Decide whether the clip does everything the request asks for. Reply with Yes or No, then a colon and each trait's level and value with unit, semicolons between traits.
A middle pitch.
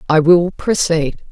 Yes: medium, 165 Hz